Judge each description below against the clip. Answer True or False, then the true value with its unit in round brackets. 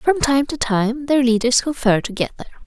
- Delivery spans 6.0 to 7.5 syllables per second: False (5.6 syllables/s)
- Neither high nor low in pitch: False (255 Hz)